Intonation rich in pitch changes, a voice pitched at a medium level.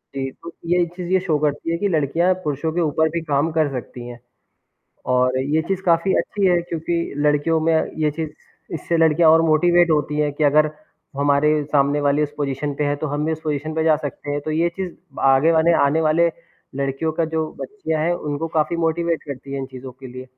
No: narrow, 2.5 semitones; medium, 155 Hz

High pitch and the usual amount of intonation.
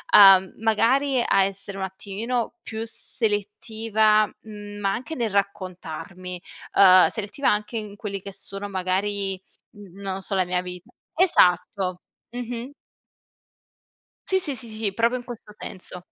Yes: high, 205 Hz; average, 3.0 semitones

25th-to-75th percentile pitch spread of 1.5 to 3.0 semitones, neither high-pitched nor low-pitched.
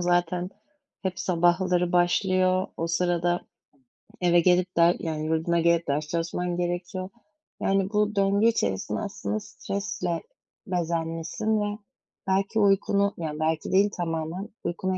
Yes: narrow, 2.4 semitones; medium, 175 Hz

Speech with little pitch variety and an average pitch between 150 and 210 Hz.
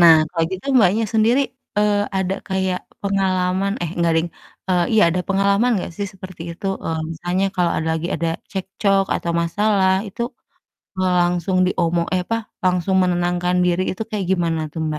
Yes: narrow, 2.1 semitones; medium, 185 Hz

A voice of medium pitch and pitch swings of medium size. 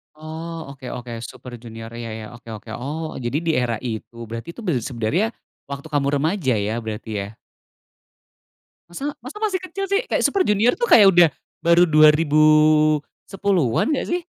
No: medium, 155 Hz; wide, 6.7 semitones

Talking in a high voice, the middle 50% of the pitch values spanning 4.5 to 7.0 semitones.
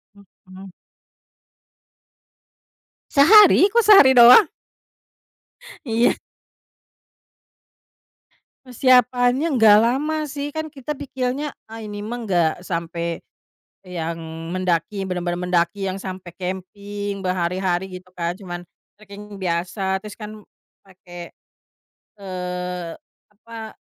Yes: high, 195 Hz; wide, 5.4 semitones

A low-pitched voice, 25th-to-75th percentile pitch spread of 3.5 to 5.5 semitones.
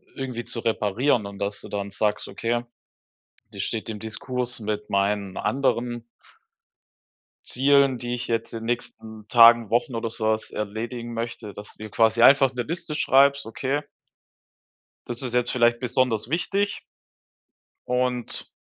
No: low, 120 Hz; narrow, 2.5 semitones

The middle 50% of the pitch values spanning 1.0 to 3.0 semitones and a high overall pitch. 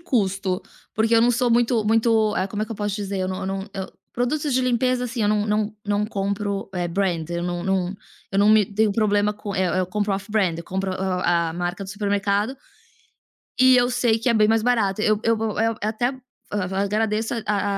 Yes: narrow, 2.6 semitones; high, 210 Hz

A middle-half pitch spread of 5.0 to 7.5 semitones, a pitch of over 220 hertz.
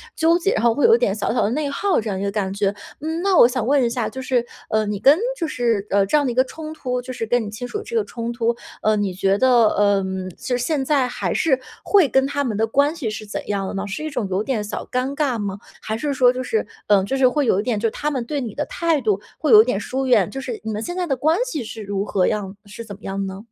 Yes: wide, 5.4 semitones; high, 245 Hz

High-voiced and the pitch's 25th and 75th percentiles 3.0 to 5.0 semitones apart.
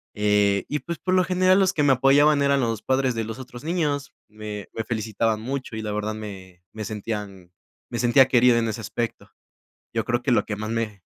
No: low, 115 Hz; average, 4.4 semitones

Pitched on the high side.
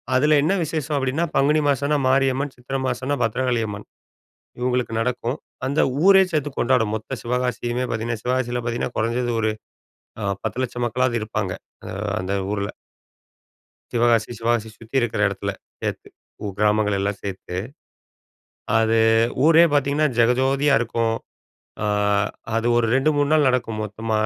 No: low, 125 Hz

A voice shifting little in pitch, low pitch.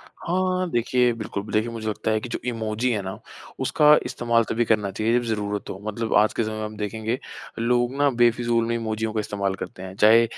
Yes: narrow, 1.8 semitones; low, 110 Hz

